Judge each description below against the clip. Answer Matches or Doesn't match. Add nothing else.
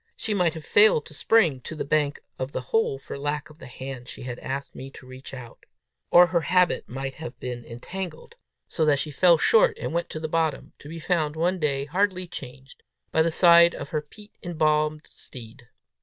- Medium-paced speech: Doesn't match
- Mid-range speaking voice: Matches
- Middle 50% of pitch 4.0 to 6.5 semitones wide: Matches